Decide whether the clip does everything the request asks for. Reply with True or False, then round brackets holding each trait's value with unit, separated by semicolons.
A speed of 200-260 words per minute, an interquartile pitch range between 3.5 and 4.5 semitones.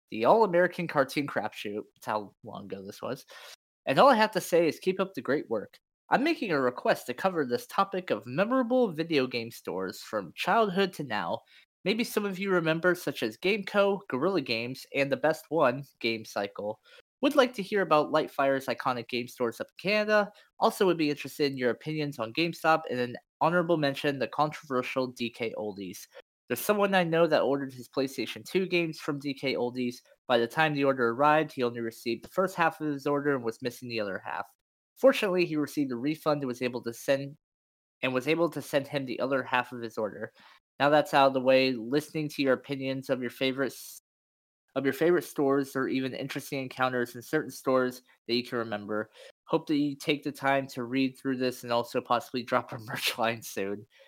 False (205 wpm; 5.1 semitones)